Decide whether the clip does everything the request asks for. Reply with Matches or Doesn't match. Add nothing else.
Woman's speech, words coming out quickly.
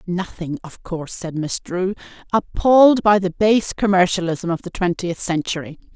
Doesn't match